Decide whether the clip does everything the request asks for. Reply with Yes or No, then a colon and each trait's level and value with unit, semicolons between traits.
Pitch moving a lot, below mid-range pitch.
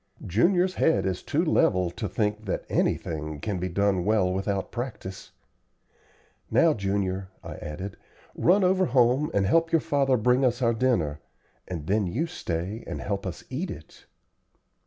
Yes: wide, 5.8 semitones; low, 105 Hz